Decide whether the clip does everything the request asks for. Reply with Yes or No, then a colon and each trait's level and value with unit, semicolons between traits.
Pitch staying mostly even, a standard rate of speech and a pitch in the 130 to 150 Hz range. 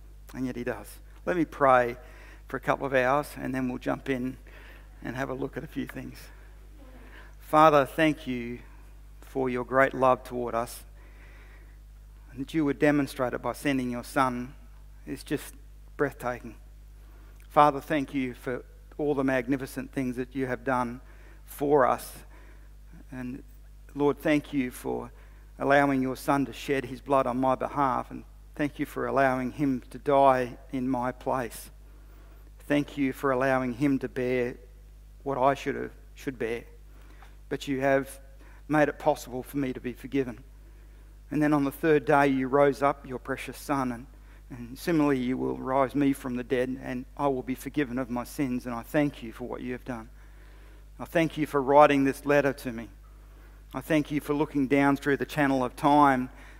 Yes: narrow, 2.1 semitones; average, 180 wpm; low, 135 Hz